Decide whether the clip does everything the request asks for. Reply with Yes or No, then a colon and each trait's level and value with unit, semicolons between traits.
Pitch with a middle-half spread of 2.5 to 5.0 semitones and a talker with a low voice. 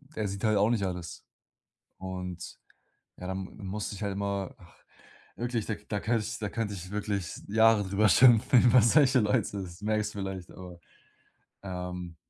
Yes: average, 2.8 semitones; low, 100 Hz